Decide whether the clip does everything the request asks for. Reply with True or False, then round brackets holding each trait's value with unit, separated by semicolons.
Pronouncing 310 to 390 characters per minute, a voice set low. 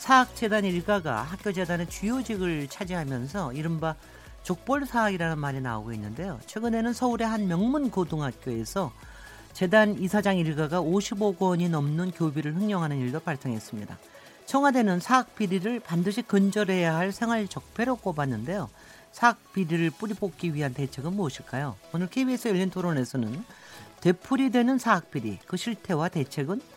False (350 characters per minute; 185 Hz)